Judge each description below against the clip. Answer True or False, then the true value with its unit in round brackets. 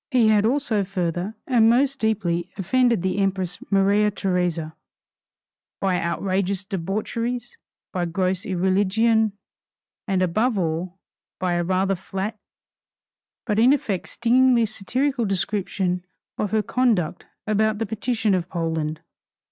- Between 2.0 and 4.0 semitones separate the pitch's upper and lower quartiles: True (3.4 semitones)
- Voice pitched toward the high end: True (195 Hz)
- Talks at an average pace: False (120 wpm)